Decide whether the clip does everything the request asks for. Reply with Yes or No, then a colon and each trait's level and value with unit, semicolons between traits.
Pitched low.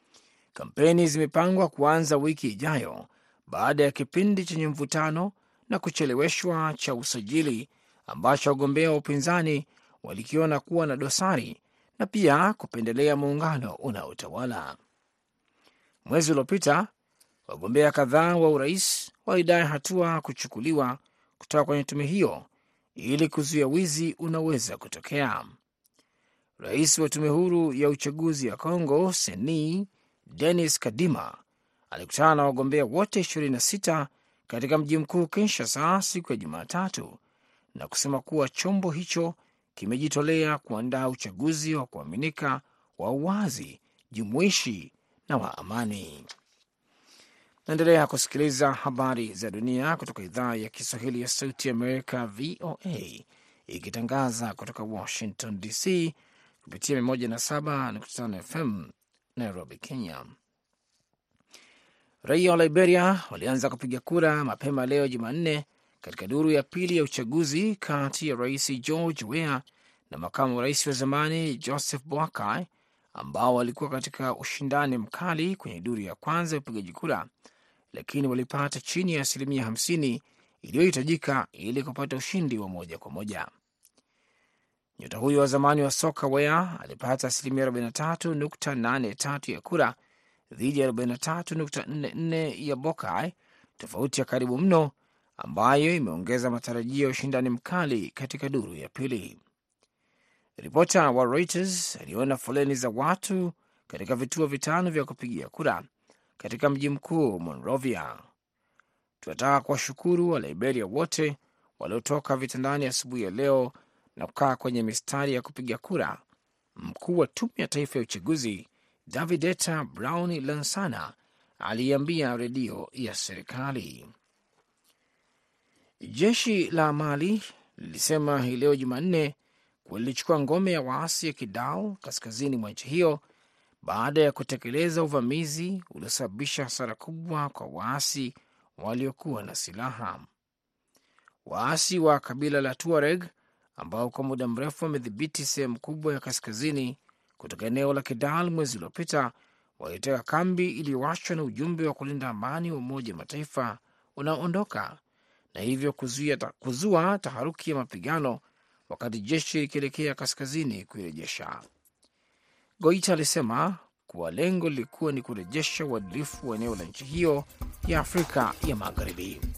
No: medium, 145 Hz